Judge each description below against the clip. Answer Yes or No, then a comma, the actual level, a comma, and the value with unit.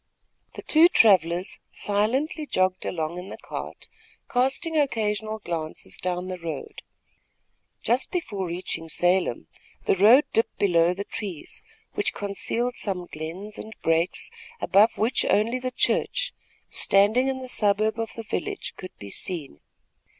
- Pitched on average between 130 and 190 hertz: No, high, 205 Hz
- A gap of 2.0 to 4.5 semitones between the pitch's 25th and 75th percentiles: No, average, 5.2 semitones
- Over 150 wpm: No, slow, 135 wpm